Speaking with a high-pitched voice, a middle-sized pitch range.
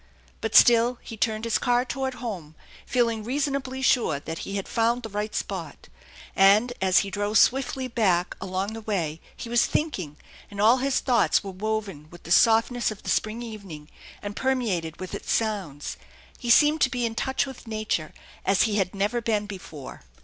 Yes: high, 215 Hz; average, 4.0 semitones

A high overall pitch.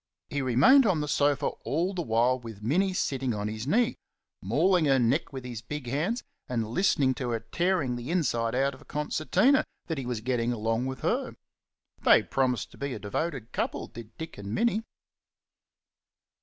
No: low, 130 Hz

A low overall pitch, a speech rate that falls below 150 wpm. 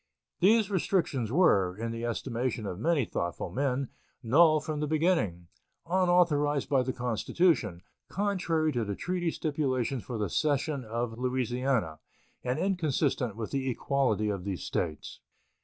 Yes: low, 130 Hz; average, 140 wpm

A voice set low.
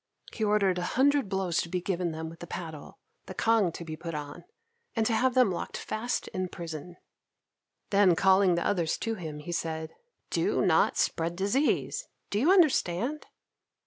No: medium, 185 Hz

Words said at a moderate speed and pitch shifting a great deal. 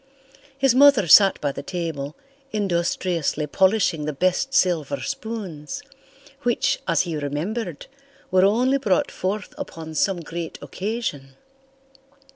No: slow, 115 wpm; wide, 5.8 semitones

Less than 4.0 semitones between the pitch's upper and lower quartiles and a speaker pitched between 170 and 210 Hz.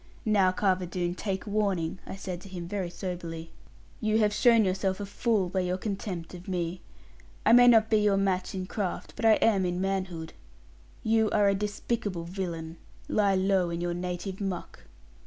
Yes: average, 2.7 semitones; high, 190 Hz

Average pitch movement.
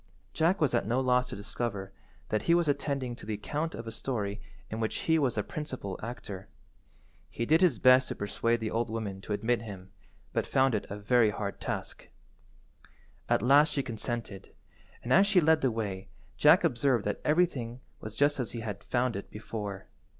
Yes: average, 4.4 semitones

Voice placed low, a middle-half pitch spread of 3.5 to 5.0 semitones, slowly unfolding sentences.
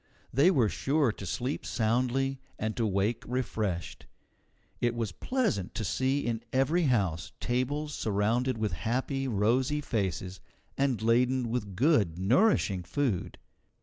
Yes: low, 120 Hz; average, 4.5 semitones; slow, 130 wpm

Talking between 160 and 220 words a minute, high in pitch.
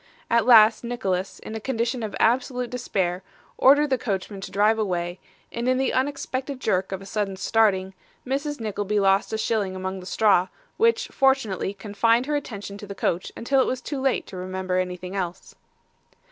Yes: average, 180 wpm; high, 215 Hz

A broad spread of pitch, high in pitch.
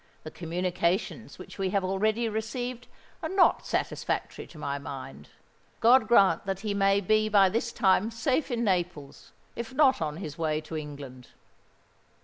Yes: wide, 6.0 semitones; high, 195 Hz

